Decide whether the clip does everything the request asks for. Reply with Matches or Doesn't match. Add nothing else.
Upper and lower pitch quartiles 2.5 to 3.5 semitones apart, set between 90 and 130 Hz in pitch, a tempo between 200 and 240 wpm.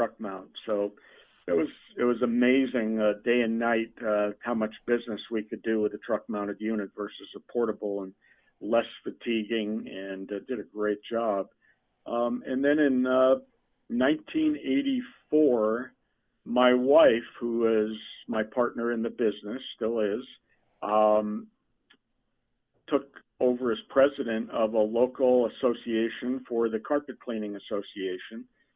Doesn't match